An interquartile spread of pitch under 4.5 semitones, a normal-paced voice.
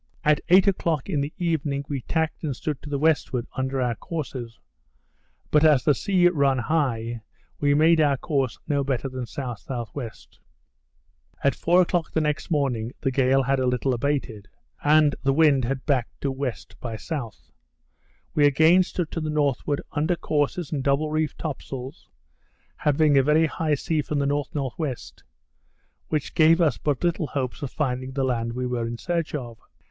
Yes: average, 3.1 semitones; average, 175 wpm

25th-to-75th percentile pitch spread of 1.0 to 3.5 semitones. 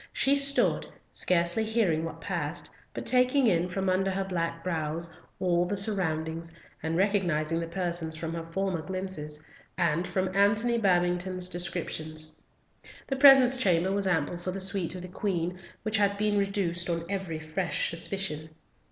Yes: average, 3.0 semitones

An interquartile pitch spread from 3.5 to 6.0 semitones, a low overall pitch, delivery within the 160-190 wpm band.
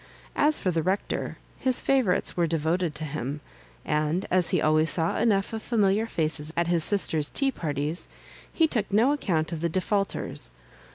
No: average, 4.9 semitones; medium, 175 Hz; average, 175 wpm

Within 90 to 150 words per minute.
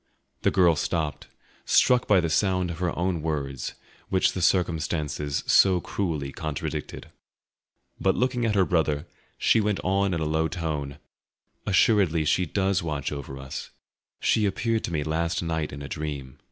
No: average, 160 wpm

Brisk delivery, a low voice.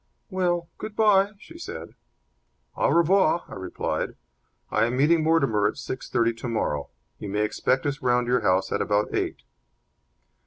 No: average, 160 wpm; low, 130 Hz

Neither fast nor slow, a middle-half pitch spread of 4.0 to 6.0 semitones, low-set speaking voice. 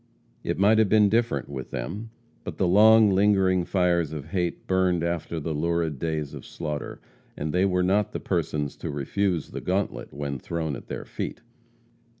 Yes: average, 175 wpm; average, 4.3 semitones; very low, 90 Hz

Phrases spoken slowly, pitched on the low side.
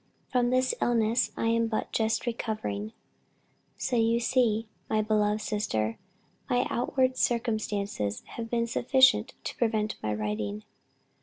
No: slow, 130 wpm; high, 225 Hz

